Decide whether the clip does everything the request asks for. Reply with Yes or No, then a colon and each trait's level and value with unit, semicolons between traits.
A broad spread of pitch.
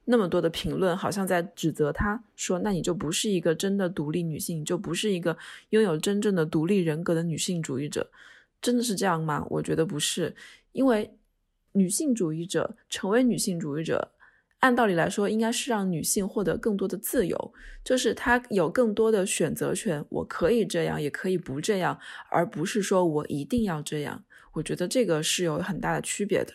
No: average, 4.9 semitones